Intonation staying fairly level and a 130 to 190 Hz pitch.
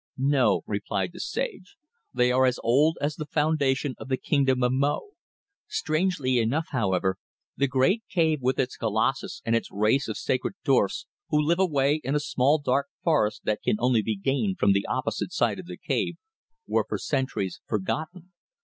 No: average, 4.8 semitones; low, 135 Hz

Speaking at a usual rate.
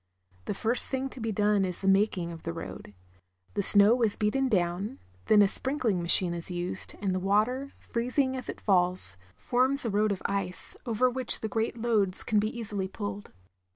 Yes: average, 190 wpm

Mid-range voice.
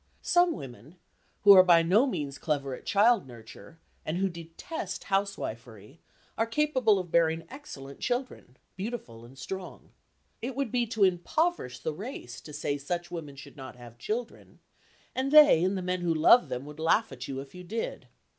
Yes: medium, 175 Hz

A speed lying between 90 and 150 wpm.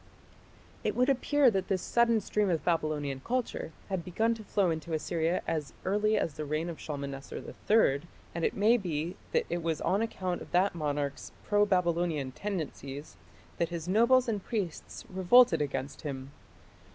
No: average, 165 wpm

